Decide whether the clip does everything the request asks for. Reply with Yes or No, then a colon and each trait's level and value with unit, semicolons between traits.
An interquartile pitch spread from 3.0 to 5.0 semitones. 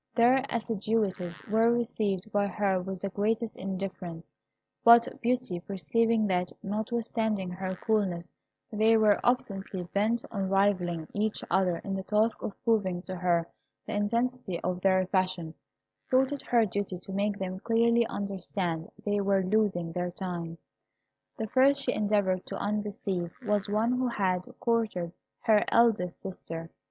Yes: average, 3.3 semitones